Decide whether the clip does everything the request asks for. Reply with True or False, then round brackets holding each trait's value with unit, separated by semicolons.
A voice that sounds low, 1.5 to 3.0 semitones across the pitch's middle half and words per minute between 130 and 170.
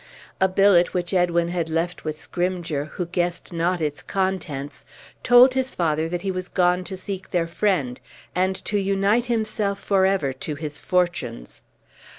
False (180 Hz; 2.7 semitones; 160 wpm)